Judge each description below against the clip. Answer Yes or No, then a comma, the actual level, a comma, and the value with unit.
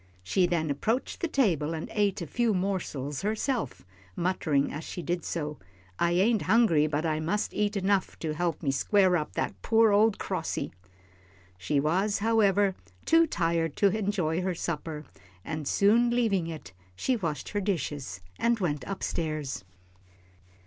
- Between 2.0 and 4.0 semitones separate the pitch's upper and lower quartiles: No, average, 5.2 semitones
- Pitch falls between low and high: Yes, medium, 180 Hz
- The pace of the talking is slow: No, average, 160 wpm